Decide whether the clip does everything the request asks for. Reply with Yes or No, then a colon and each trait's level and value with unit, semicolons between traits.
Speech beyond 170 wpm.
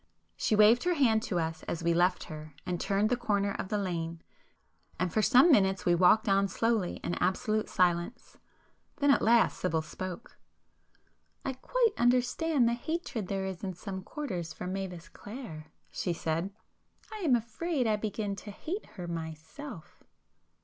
No: average, 155 wpm